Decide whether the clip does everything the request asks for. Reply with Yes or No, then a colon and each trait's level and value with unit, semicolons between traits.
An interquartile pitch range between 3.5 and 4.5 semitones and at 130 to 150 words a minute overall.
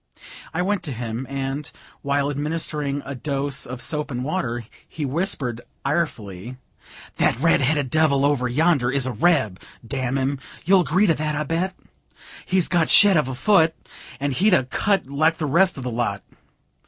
No: average, 4.1 semitones; average, 175 wpm